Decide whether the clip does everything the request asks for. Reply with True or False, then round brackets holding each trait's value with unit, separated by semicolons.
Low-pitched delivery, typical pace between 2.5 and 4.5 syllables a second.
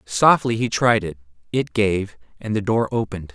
False (105 Hz; 4.9 syllables/s)